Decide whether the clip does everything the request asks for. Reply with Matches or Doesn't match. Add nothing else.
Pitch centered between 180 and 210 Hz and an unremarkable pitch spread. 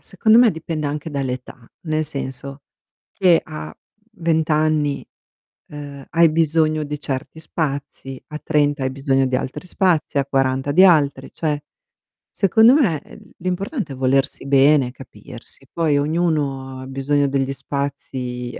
Doesn't match